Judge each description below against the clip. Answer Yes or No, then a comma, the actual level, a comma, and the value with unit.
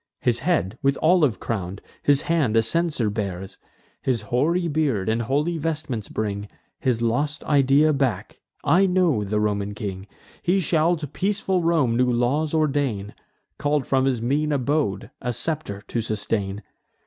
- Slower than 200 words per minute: Yes, average, 150 wpm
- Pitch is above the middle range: No, low, 130 Hz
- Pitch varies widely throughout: Yes, wide, 6.4 semitones